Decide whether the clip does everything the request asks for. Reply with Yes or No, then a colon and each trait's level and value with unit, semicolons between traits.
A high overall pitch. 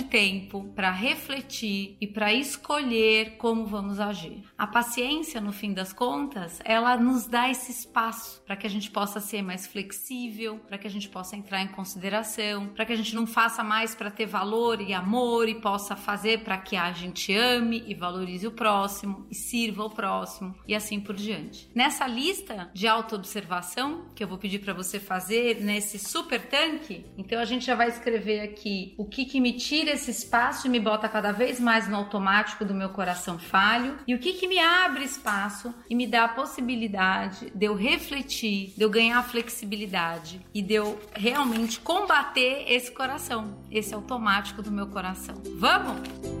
Yes: high, 220 Hz